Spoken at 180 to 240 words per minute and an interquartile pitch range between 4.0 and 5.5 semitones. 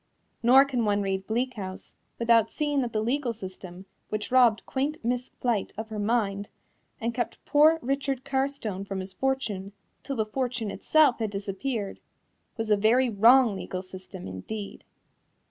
No: average, 160 wpm; average, 4.5 semitones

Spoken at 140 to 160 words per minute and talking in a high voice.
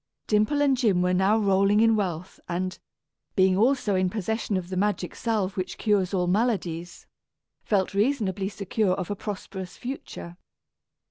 Yes: average, 150 wpm; high, 195 Hz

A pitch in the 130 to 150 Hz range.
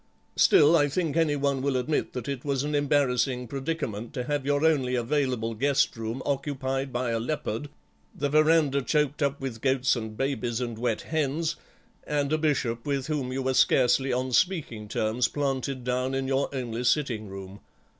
Yes: low, 135 Hz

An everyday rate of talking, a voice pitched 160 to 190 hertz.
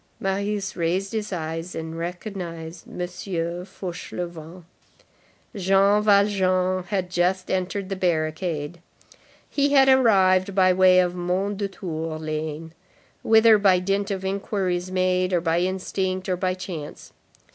No: slow, 115 wpm; medium, 185 Hz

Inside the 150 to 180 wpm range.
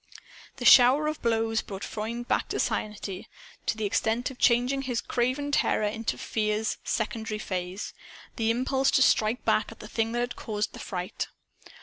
Yes: average, 170 wpm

